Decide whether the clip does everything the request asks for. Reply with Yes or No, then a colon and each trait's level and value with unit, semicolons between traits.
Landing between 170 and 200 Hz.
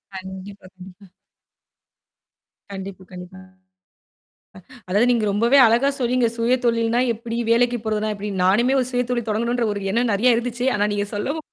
No: high, 230 Hz